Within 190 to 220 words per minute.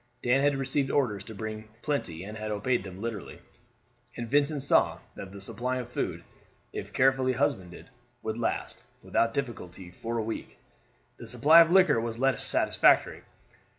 No: average, 160 wpm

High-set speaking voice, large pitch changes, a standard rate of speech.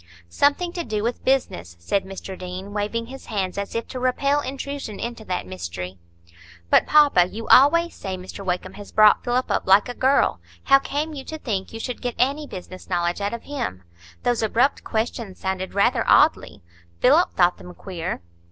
Yes: high, 220 Hz; wide, 6.3 semitones; average, 185 wpm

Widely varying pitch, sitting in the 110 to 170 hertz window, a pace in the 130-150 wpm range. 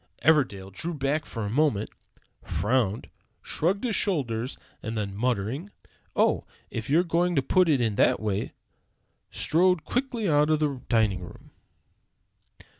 Yes: wide, 7.3 semitones; low, 135 Hz; average, 140 wpm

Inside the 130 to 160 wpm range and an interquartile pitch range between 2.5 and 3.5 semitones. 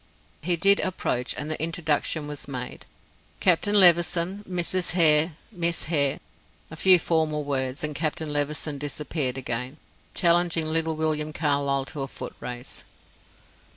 Yes: average, 140 wpm; average, 3.0 semitones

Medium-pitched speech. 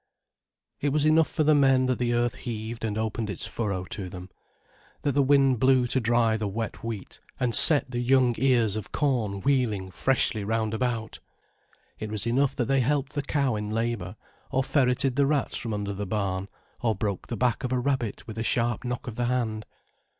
No: low, 120 Hz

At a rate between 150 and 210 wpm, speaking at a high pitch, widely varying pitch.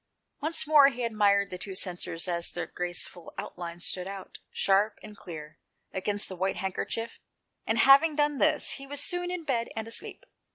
Yes: average, 175 wpm; high, 205 Hz; wide, 7.0 semitones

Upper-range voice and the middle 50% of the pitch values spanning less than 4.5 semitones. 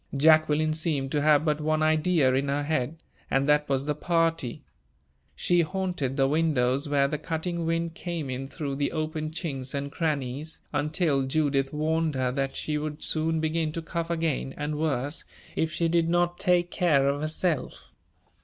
No: medium, 155 Hz; average, 2.8 semitones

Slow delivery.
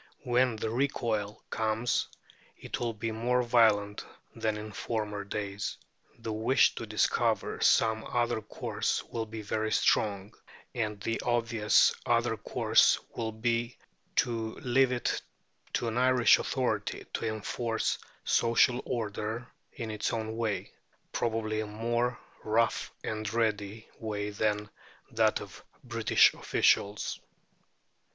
Yes: slow, 125 wpm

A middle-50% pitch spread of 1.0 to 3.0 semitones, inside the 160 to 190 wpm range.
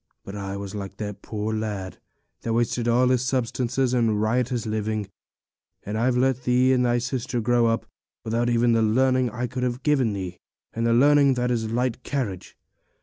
Yes: narrow, 2.6 semitones; average, 175 wpm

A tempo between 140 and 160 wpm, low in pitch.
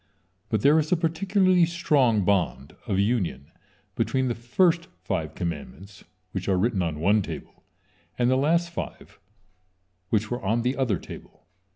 Yes: average, 155 wpm; low, 120 Hz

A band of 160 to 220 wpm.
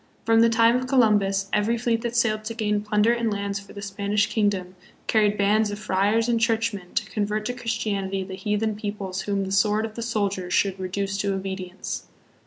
Yes: average, 195 wpm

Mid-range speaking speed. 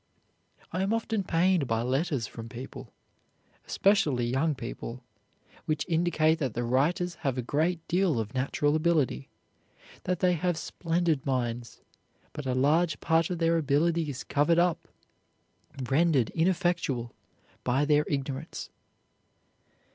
No: slow, 130 wpm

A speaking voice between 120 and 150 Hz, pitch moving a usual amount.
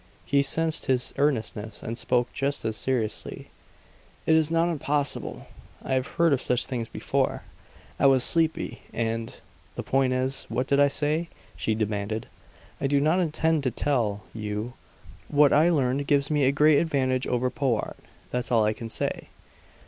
Yes: low, 135 Hz; average, 3.9 semitones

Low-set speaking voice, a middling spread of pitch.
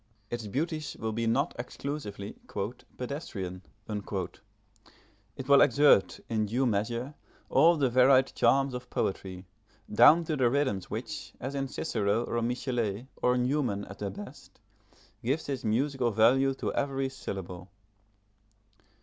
Yes: low, 120 Hz; average, 4.8 semitones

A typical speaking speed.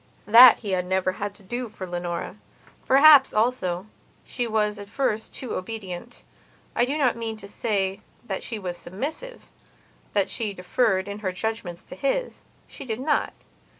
Yes: average, 160 wpm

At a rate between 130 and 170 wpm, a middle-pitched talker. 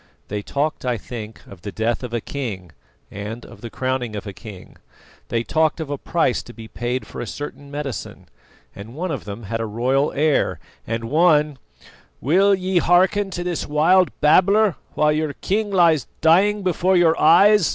No: average, 185 wpm; medium, 145 Hz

